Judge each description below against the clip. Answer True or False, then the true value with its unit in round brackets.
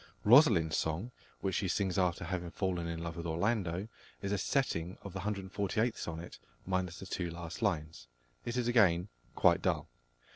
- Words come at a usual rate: True (170 wpm)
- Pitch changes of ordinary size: True (3.4 semitones)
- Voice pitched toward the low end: True (95 Hz)